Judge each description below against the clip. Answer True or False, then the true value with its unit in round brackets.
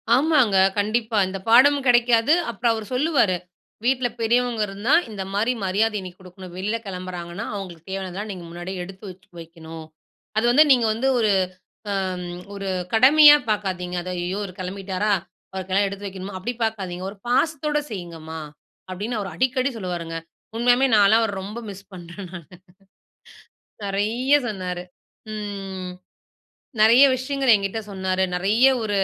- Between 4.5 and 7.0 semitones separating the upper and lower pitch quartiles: False (4.1 semitones)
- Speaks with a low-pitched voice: False (200 Hz)